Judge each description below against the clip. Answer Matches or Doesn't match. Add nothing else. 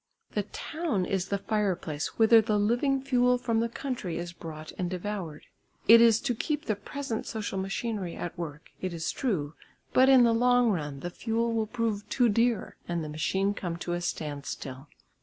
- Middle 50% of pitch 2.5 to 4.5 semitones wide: Doesn't match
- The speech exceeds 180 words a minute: Matches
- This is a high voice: Matches